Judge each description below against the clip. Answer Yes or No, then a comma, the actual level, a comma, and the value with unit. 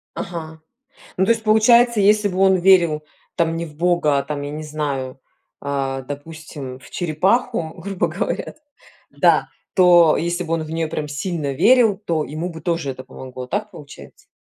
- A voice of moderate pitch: Yes, medium, 165 Hz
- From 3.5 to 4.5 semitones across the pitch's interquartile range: Yes, average, 4.2 semitones